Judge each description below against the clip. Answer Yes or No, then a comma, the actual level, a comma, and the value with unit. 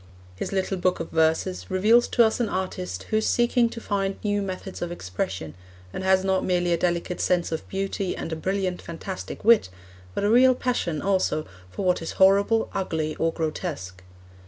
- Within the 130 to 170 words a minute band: No, average, 185 wpm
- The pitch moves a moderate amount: Yes, average, 3.2 semitones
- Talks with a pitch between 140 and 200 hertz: Yes, medium, 185 Hz